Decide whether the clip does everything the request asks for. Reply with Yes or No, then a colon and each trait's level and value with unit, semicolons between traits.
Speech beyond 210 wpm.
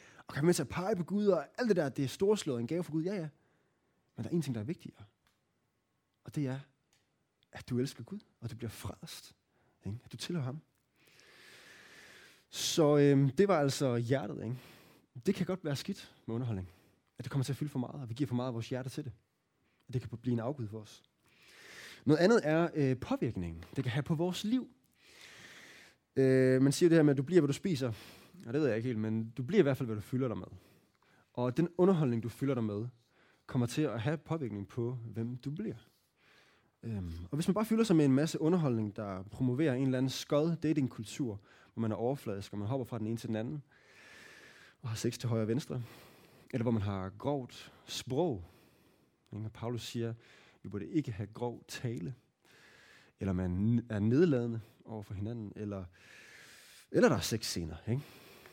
Yes: average, 220 wpm